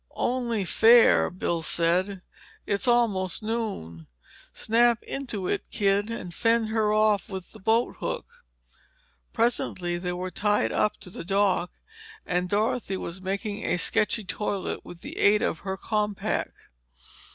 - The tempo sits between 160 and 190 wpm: No, slow, 135 wpm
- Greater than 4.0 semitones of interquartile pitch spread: No, average, 3.4 semitones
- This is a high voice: Yes, high, 205 Hz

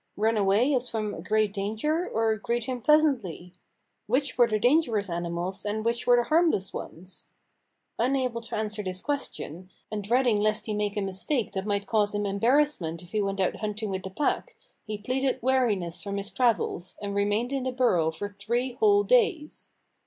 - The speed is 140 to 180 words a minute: No, average, 195 wpm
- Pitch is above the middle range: Yes, high, 215 Hz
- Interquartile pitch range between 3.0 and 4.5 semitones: Yes, average, 4.1 semitones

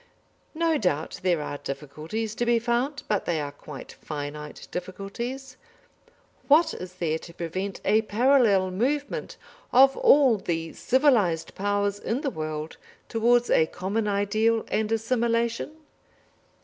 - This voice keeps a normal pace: No, slow, 130 wpm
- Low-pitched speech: No, high, 210 Hz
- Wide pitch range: Yes, wide, 6.0 semitones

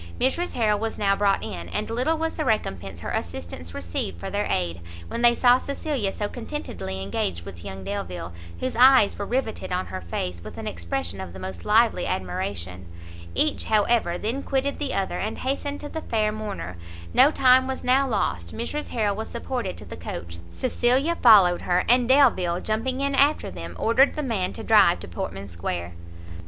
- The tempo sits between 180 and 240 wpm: Yes, average, 190 wpm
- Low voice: No, high, 205 Hz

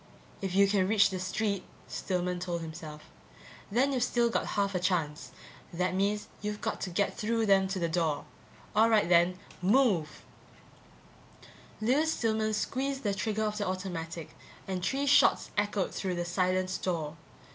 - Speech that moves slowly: No, average, 160 wpm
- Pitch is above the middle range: Yes, high, 195 Hz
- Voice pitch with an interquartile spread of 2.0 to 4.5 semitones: Yes, average, 3.3 semitones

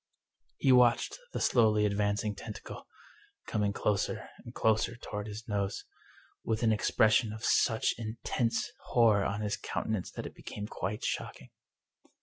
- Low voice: Yes, low, 110 Hz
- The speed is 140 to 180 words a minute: Yes, average, 145 wpm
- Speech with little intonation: Yes, narrow, 1.6 semitones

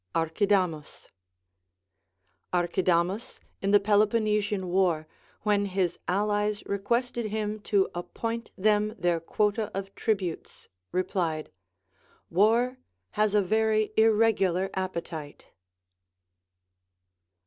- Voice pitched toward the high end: Yes, high, 200 Hz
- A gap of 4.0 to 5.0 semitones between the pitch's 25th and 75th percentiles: No, average, 2.9 semitones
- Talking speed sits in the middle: No, slow, 85 wpm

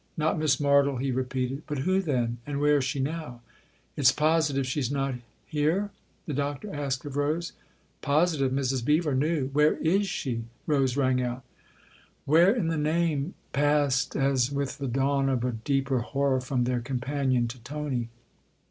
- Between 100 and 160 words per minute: No, average, 190 wpm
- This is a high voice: No, medium, 140 Hz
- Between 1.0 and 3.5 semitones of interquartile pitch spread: Yes, narrow, 2.5 semitones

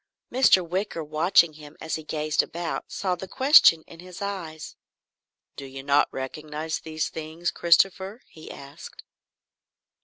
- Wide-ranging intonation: No, average, 3.0 semitones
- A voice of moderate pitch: Yes, medium, 160 Hz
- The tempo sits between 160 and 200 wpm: No, slow, 135 wpm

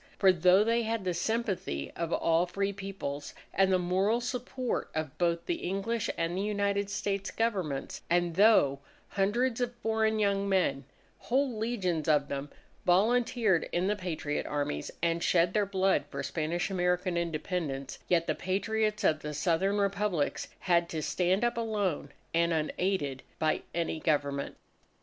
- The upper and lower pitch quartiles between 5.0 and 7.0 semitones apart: No, average, 4.0 semitones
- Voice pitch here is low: No, medium, 185 Hz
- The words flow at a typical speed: Yes, average, 155 wpm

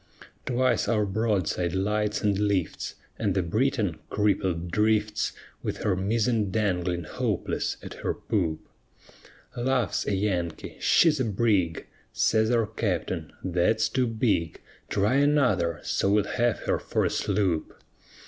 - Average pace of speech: No, slow, 130 wpm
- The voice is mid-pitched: No, low, 105 Hz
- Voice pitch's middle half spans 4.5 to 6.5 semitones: No, average, 3.7 semitones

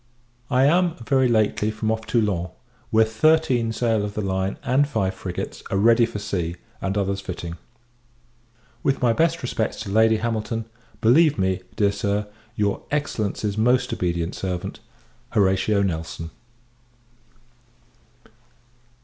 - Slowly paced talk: Yes, slow, 130 wpm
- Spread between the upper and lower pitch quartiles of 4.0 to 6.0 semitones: No, average, 3.3 semitones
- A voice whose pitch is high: No, low, 110 Hz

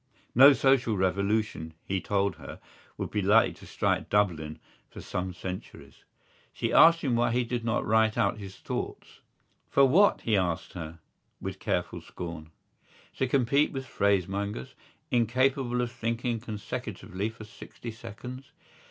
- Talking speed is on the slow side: No, average, 145 wpm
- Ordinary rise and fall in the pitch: Yes, average, 4.2 semitones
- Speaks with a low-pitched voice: Yes, low, 110 Hz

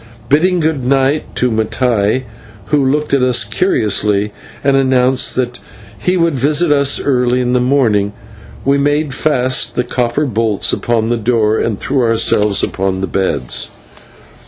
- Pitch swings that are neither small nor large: Yes, average, 4.1 semitones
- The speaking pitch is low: Yes, low, 125 Hz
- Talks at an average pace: Yes, average, 150 wpm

